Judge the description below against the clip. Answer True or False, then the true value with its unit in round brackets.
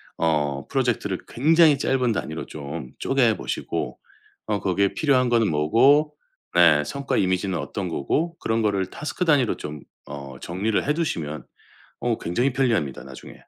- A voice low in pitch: True (105 Hz)